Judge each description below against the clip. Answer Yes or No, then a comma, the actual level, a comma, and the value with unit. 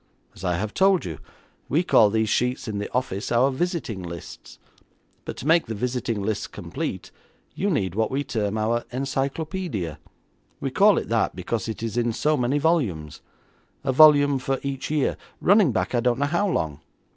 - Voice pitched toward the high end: No, low, 125 Hz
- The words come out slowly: No, average, 180 wpm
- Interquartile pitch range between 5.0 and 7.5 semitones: Yes, wide, 5.4 semitones